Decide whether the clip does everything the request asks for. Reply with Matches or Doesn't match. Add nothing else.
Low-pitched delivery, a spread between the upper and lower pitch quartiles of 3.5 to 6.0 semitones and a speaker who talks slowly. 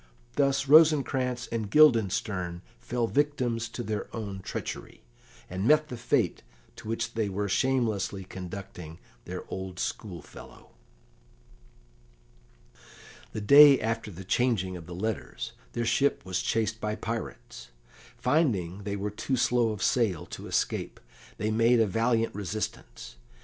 Matches